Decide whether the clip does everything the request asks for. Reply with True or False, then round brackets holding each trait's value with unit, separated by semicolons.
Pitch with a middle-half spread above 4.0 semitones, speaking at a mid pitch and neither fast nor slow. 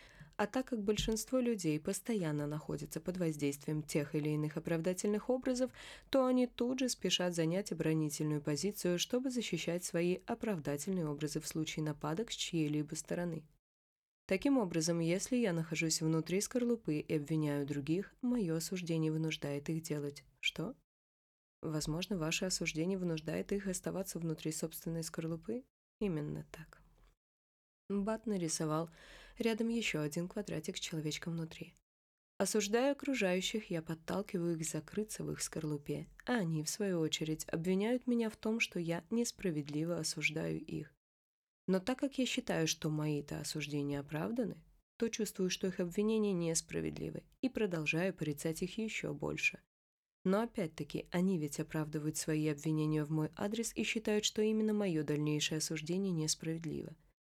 True (5.1 semitones; 170 Hz; 135 wpm)